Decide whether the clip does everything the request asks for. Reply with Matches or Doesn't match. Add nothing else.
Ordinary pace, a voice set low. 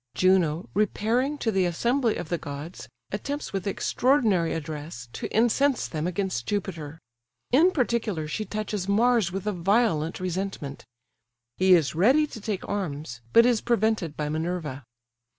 Doesn't match